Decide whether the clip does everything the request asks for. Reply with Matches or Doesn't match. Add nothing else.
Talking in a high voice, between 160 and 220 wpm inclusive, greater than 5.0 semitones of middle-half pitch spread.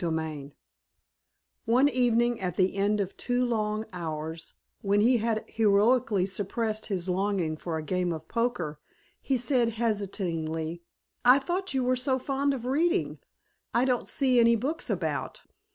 Doesn't match